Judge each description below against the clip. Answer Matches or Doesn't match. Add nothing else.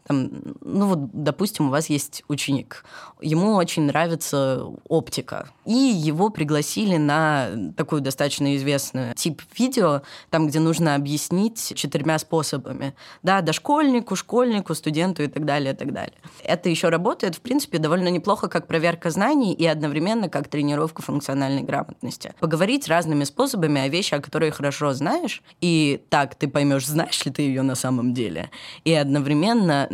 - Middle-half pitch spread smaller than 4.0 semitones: Matches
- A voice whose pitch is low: Doesn't match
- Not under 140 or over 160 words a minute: Matches